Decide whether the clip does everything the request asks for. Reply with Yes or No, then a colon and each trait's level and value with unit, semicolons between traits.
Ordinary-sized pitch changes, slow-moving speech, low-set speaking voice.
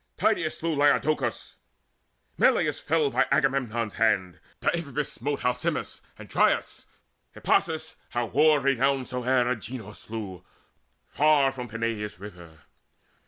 Yes: average, 4.3 semitones; slow, 110 wpm; low, 125 Hz